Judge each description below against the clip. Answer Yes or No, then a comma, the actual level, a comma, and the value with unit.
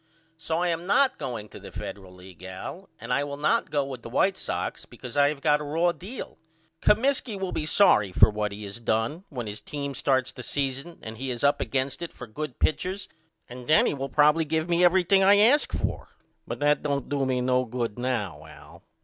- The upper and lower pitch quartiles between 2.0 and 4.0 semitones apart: No, wide, 5.6 semitones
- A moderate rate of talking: No, fast, 225 wpm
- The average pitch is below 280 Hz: Yes, medium, 140 Hz